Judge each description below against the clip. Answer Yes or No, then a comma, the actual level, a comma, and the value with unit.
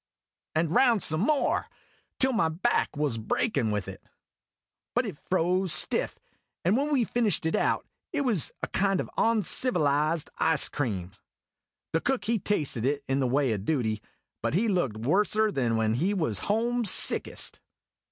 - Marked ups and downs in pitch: Yes, wide, 8.3 semitones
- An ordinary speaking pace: Yes, average, 160 wpm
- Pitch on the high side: No, medium, 165 Hz